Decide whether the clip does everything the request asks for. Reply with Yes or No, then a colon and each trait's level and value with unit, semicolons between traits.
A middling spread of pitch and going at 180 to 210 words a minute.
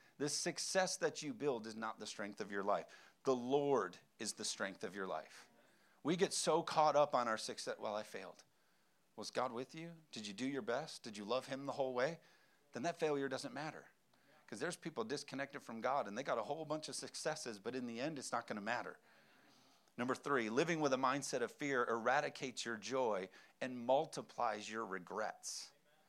Yes: average, 4.4 semitones; fast, 205 wpm